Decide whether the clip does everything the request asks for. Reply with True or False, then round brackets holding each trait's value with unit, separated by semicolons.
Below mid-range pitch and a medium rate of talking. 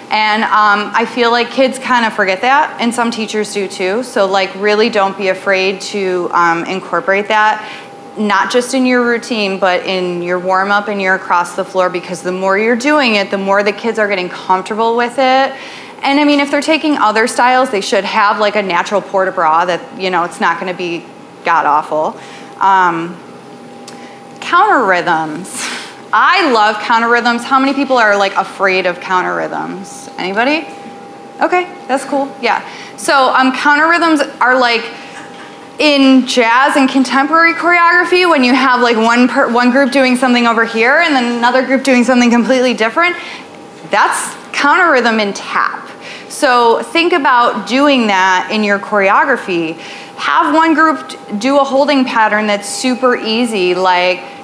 False (230 Hz; 170 wpm)